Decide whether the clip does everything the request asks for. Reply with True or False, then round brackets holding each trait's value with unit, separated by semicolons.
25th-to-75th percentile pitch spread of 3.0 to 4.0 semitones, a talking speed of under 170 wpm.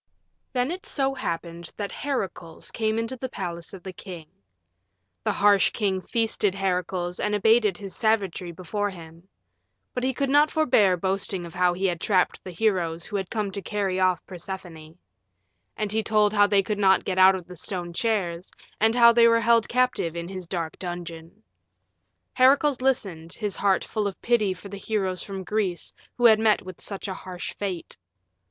False (3.6 semitones; 185 wpm)